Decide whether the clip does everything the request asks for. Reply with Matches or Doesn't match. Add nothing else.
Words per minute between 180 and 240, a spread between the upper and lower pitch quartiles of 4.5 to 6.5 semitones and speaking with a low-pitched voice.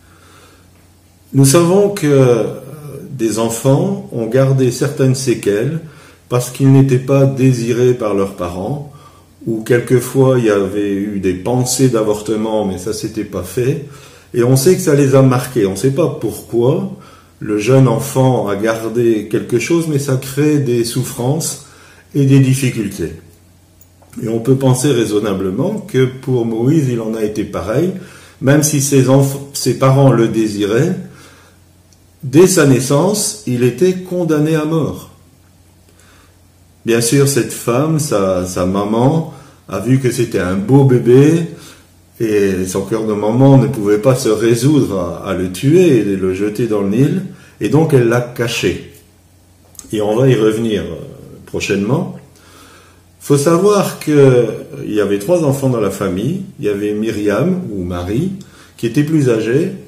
Doesn't match